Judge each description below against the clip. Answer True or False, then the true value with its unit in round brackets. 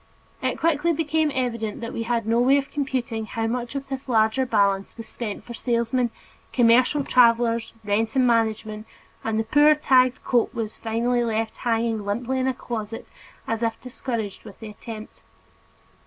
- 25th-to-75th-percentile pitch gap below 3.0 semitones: True (2.4 semitones)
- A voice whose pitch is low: False (235 Hz)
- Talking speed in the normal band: True (170 wpm)